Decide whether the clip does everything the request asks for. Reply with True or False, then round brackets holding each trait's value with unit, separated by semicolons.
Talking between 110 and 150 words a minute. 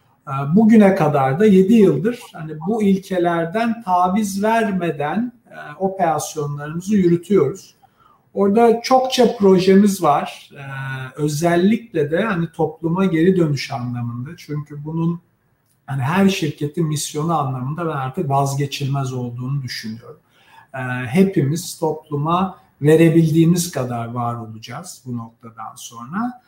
False (100 wpm)